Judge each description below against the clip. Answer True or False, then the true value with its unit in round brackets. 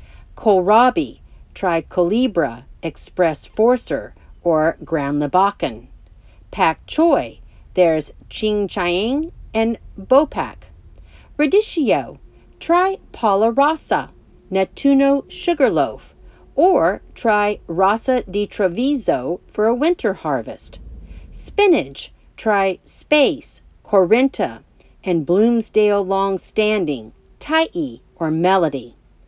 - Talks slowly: True (80 wpm)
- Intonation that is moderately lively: False (6.9 semitones)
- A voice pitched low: False (210 Hz)